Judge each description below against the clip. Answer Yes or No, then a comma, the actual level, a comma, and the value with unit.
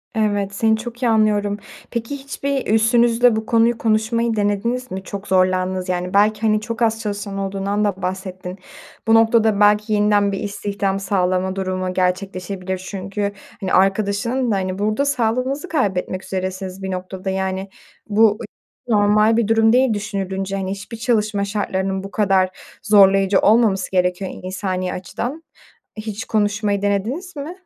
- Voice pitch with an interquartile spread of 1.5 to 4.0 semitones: Yes, average, 2.7 semitones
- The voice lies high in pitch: Yes, high, 205 Hz